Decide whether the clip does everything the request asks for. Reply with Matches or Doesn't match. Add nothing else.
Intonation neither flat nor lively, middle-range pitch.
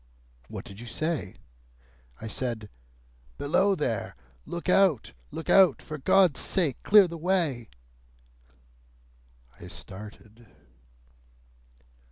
Doesn't match